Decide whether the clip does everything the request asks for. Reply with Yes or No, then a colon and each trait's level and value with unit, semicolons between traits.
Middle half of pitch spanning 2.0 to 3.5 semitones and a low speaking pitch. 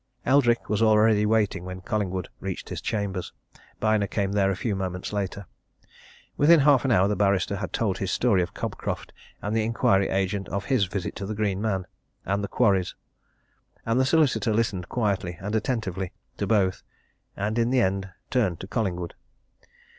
Yes: average, 2.8 semitones; low, 100 Hz